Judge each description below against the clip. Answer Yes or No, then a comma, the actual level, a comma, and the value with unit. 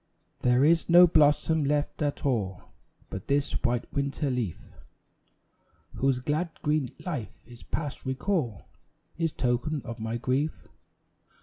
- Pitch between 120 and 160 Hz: Yes, medium, 140 Hz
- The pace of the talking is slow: Yes, slow, 125 wpm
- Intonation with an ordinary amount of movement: Yes, average, 3.8 semitones